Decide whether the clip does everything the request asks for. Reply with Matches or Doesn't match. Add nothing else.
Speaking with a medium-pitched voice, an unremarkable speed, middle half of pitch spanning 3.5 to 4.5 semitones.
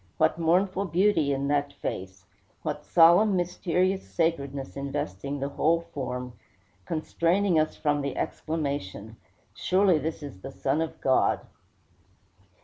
Doesn't match